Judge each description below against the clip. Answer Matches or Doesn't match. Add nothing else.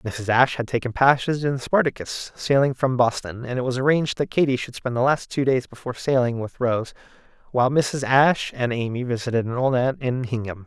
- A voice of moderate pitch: Doesn't match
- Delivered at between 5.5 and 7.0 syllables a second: Matches